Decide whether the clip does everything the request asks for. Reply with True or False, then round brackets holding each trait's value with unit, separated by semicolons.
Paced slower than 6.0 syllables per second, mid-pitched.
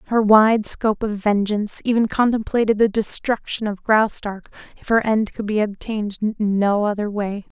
False (5.0 syllables/s; 210 Hz)